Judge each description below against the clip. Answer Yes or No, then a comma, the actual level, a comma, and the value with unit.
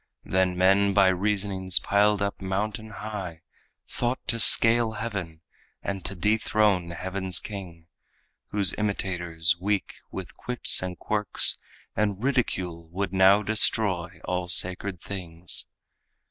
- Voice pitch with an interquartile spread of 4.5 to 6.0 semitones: No, narrow, 2.6 semitones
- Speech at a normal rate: No, slow, 120 wpm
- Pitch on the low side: Yes, very low, 95 Hz